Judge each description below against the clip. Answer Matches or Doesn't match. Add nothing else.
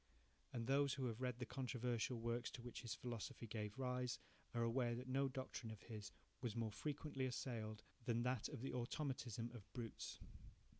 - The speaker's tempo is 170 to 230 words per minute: Matches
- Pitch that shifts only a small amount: Matches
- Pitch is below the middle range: Matches